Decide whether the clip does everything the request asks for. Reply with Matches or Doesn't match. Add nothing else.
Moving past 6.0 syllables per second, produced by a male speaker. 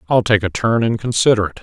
Matches